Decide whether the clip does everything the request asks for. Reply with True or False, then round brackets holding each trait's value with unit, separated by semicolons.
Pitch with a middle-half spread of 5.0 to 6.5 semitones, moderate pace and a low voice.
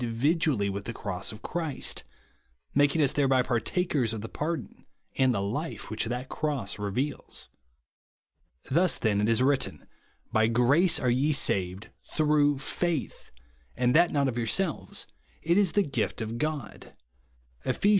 True (5.3 semitones; 150 wpm; 130 Hz)